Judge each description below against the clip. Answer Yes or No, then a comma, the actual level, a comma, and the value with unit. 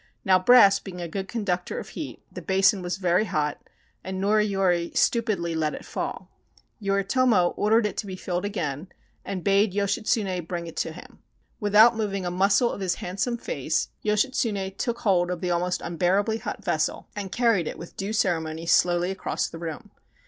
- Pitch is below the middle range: No, high, 195 Hz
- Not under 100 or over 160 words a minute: No, average, 185 wpm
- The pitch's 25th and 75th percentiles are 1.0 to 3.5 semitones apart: Yes, average, 3.0 semitones